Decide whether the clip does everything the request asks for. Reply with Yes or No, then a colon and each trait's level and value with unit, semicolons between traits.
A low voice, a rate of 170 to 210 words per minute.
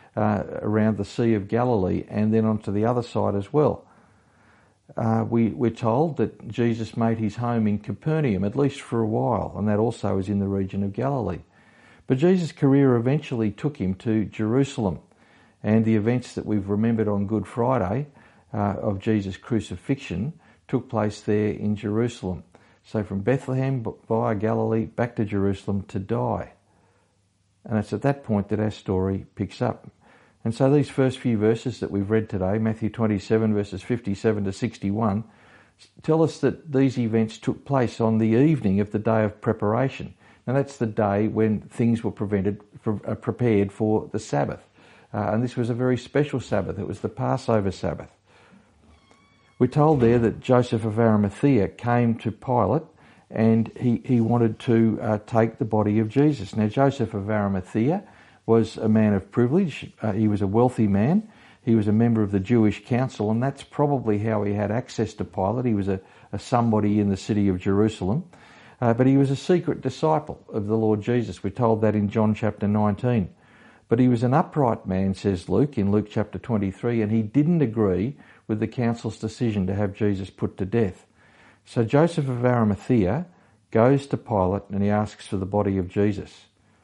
Yes: low, 110 Hz; average, 185 wpm